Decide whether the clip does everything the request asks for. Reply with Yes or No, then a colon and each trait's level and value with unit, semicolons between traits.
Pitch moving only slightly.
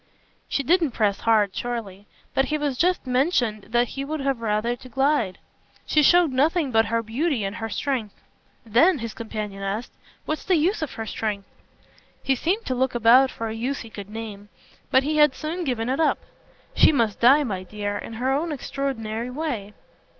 No: average, 4.7 semitones